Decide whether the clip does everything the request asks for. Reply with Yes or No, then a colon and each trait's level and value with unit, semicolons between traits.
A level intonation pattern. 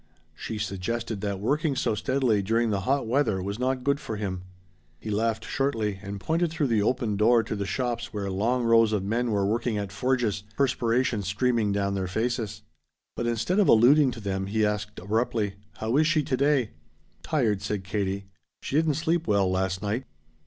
No: average, 3.9 semitones